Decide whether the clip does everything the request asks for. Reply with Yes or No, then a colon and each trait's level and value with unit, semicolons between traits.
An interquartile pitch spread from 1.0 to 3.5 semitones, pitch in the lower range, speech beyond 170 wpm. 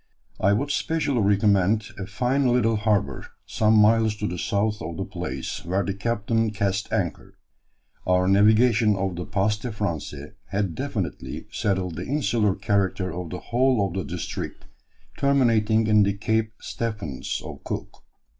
No: average, 2.9 semitones; low, 105 Hz; average, 155 wpm